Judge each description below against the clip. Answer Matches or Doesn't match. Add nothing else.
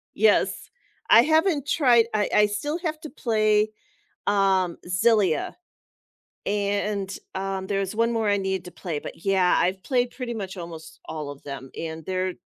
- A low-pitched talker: Doesn't match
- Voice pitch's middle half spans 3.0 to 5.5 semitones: Matches